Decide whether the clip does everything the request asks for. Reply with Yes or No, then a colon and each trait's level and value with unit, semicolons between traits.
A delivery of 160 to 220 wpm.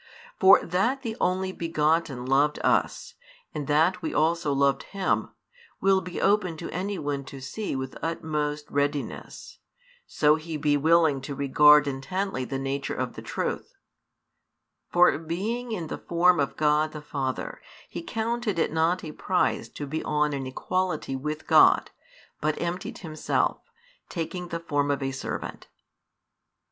No: average, 150 wpm